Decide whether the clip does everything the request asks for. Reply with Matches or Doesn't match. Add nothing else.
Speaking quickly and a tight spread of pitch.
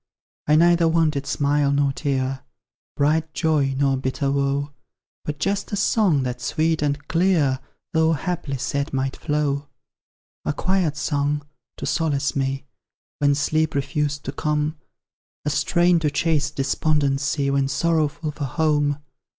Doesn't match